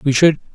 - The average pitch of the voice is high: No, medium, 145 Hz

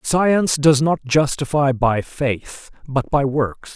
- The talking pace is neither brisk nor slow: Yes, average, 145 wpm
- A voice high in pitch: No, medium, 140 Hz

